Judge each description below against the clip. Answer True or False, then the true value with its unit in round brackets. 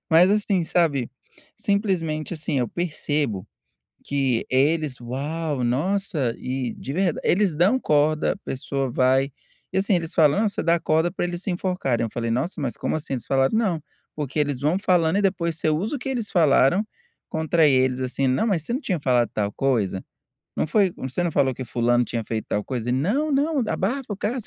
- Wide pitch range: True (6.0 semitones)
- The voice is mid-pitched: True (155 Hz)